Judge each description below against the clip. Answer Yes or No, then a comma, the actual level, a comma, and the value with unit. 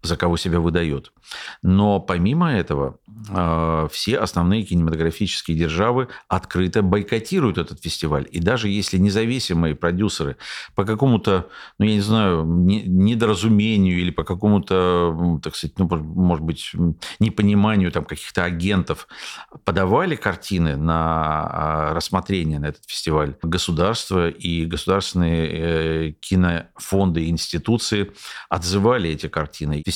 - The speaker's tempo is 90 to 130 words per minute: Yes, slow, 110 wpm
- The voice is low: Yes, very low, 90 Hz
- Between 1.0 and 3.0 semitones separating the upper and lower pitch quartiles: No, average, 3.6 semitones